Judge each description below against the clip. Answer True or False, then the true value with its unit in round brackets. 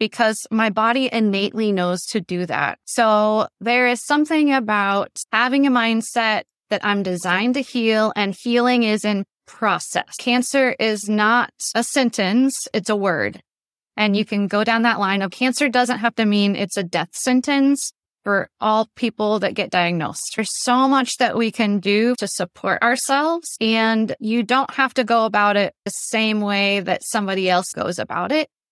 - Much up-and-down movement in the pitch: False (3.4 semitones)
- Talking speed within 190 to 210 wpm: False (175 wpm)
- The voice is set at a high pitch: True (220 Hz)